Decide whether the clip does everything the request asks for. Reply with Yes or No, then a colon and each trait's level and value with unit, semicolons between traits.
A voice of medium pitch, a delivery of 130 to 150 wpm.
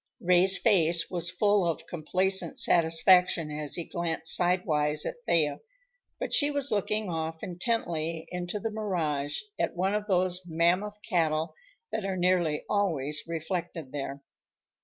Yes: medium, 175 Hz; average, 140 wpm